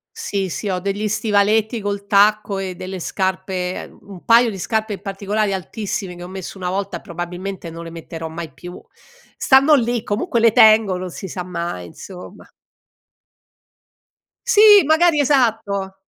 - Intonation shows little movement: No, average, 3.2 semitones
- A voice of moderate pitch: No, high, 195 Hz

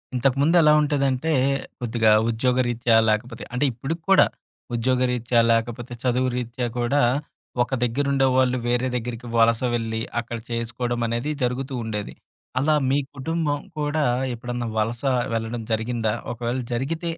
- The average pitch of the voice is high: No, low, 125 Hz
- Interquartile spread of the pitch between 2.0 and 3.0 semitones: Yes, narrow, 2.5 semitones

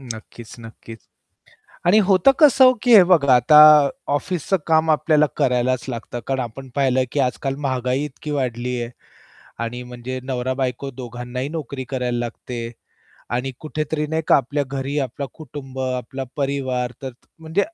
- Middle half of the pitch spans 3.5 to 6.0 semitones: No, average, 3.1 semitones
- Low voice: Yes, low, 130 Hz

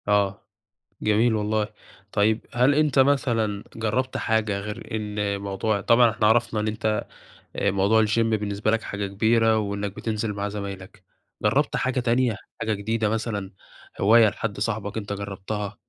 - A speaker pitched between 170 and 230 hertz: No, low, 105 Hz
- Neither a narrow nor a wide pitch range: No, narrow, 1.8 semitones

